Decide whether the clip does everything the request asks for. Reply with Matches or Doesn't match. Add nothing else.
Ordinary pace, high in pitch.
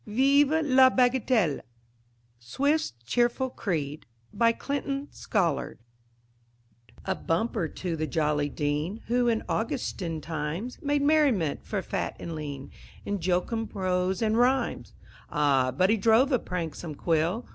Doesn't match